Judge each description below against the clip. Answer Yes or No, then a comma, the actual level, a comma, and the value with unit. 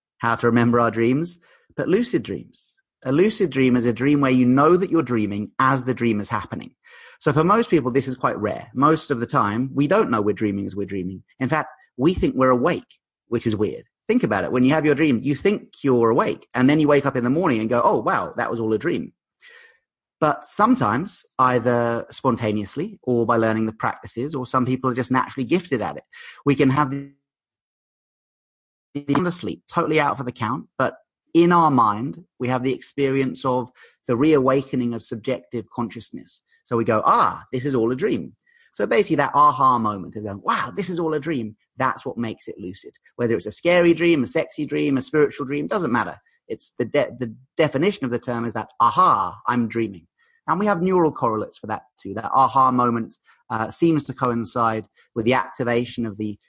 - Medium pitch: No, low, 130 Hz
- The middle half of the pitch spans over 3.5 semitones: Yes, average, 4.5 semitones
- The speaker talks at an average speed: No, fast, 210 wpm